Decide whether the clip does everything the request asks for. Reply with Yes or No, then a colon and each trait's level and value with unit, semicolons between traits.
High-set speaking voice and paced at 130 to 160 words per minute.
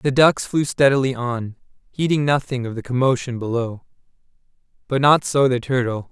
No: low, 130 Hz; average, 155 wpm